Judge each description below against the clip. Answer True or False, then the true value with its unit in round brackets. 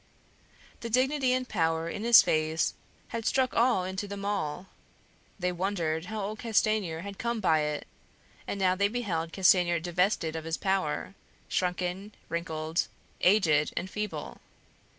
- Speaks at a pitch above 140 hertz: True (190 Hz)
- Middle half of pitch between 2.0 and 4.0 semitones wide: False (4.5 semitones)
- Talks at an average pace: True (145 wpm)